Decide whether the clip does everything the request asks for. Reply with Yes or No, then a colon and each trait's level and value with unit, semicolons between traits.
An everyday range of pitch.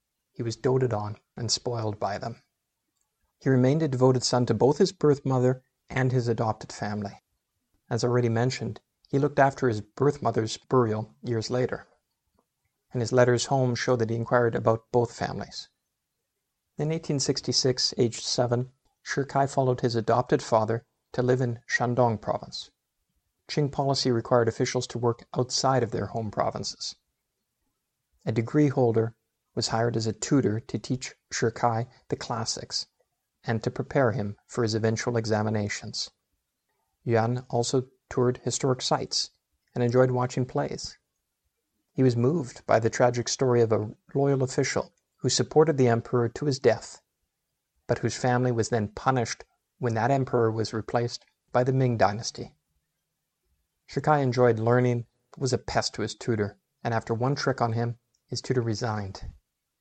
No: narrow, 2.2 semitones